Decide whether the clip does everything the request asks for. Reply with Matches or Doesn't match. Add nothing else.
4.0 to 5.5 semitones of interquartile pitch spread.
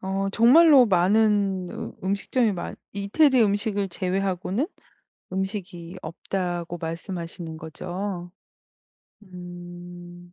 Doesn't match